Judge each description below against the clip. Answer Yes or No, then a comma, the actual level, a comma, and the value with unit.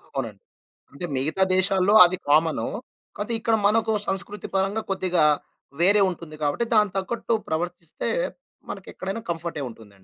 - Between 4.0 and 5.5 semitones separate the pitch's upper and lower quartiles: Yes, average, 4.6 semitones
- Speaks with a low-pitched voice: No, medium, 185 Hz